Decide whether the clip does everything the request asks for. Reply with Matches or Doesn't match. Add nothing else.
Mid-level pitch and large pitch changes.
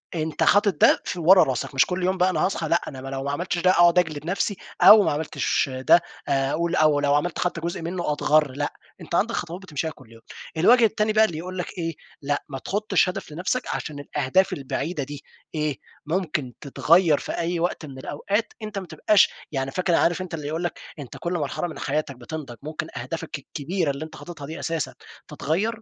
Doesn't match